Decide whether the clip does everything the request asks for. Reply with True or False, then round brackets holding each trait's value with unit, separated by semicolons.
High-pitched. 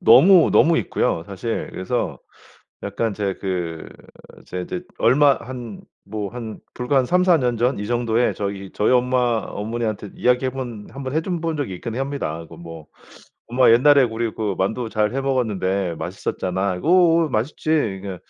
False (115 Hz)